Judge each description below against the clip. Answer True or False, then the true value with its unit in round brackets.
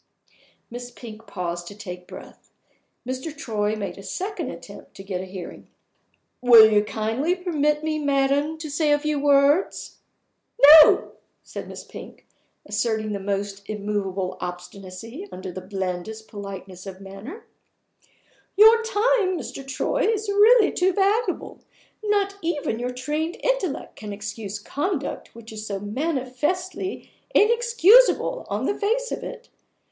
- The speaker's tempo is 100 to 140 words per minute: True (135 wpm)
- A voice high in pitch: True (260 Hz)